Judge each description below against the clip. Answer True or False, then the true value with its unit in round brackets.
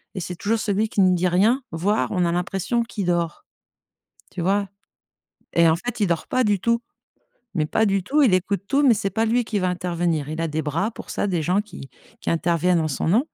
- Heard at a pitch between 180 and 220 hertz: True (185 Hz)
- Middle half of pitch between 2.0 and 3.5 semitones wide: False (4.1 semitones)